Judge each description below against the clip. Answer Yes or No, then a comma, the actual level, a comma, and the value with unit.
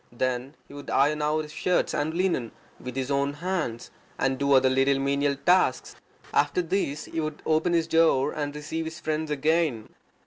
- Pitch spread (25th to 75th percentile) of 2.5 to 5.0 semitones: Yes, average, 2.8 semitones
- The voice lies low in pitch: No, medium, 150 Hz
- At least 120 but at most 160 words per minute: No, average, 180 wpm